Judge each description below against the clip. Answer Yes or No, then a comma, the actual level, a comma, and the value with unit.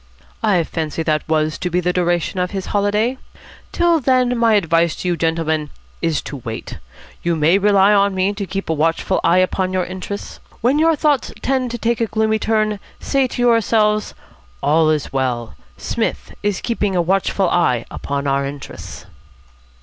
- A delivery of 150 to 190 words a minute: Yes, average, 175 wpm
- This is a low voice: No, medium, 185 Hz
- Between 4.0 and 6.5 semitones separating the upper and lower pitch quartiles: Yes, average, 5.1 semitones